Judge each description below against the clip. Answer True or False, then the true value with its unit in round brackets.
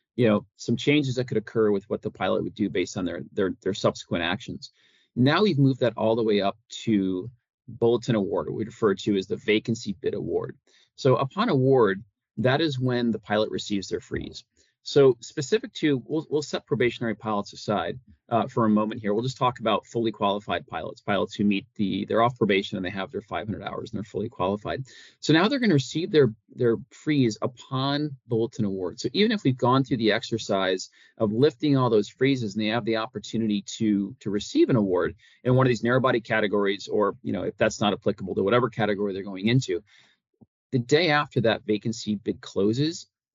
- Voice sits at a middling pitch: False (115 Hz)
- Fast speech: True (210 wpm)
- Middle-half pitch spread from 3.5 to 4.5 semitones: True (3.9 semitones)